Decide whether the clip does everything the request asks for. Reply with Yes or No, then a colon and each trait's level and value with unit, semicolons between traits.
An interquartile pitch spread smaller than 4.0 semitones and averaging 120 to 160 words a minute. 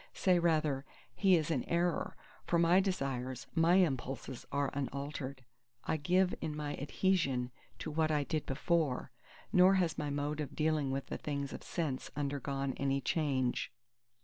Yes: average, 3.5 semitones; average, 155 wpm